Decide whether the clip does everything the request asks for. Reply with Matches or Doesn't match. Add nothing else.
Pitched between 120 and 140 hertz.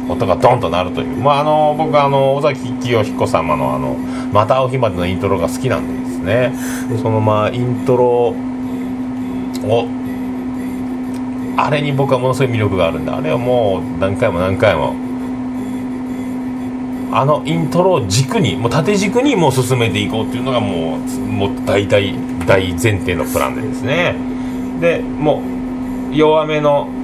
Matches